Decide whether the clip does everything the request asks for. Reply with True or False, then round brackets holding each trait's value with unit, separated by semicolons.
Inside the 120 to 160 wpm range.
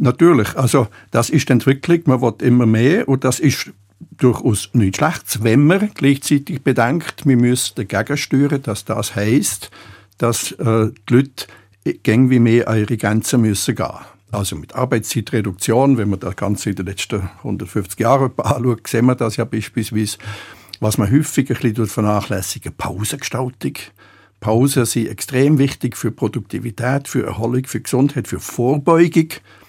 True (150 wpm)